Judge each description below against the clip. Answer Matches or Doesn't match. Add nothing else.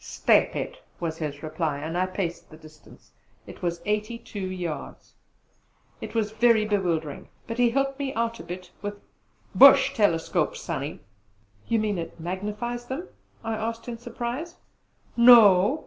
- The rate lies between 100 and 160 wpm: Matches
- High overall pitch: Matches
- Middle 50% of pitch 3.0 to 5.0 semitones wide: Doesn't match